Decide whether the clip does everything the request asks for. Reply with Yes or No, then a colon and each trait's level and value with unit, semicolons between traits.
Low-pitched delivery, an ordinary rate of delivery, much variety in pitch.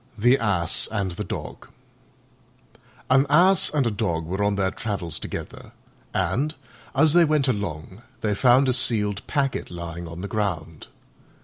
Yes: low, 105 Hz; average, 150 wpm; wide, 7.0 semitones